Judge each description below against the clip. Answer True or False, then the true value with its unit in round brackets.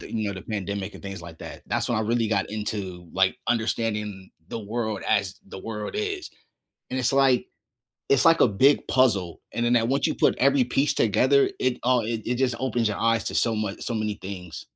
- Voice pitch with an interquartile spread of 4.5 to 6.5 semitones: False (3.7 semitones)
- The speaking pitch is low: True (110 Hz)